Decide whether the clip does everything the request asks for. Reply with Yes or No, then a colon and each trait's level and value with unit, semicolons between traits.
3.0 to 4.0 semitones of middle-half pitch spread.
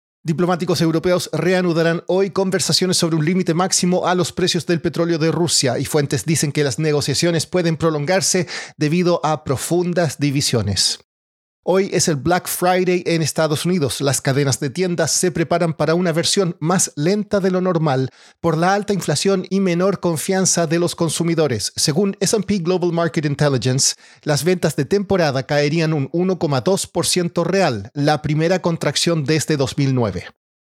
Yes: average, 3.3 semitones